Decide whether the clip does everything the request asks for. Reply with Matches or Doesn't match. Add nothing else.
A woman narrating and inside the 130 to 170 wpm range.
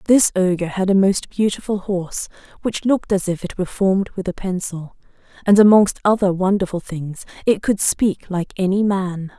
Doesn't match